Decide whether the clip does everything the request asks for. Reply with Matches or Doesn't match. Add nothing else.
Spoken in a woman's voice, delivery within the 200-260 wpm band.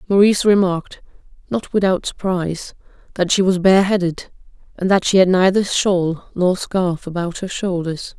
Doesn't match